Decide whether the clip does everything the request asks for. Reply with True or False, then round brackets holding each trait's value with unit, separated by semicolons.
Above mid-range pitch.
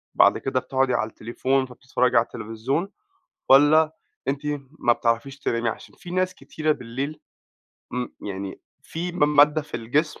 False (135 Hz)